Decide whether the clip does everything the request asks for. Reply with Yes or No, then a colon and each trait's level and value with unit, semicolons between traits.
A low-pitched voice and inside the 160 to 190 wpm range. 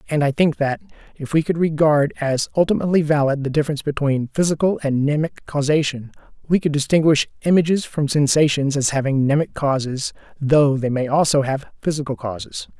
No: medium, 145 Hz; average, 165 wpm